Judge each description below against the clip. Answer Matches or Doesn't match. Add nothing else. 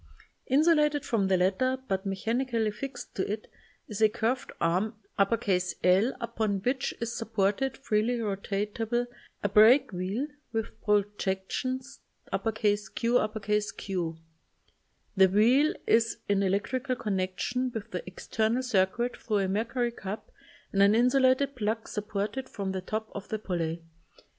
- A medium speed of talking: Doesn't match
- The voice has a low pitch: Doesn't match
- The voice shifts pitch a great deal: Doesn't match